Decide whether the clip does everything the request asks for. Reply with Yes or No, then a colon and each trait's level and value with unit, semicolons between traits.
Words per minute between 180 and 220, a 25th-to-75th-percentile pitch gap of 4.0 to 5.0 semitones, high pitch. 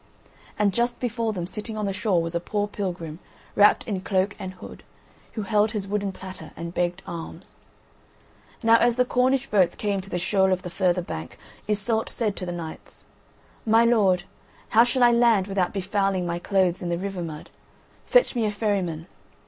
No: average, 190 wpm; average, 3.4 semitones; high, 195 Hz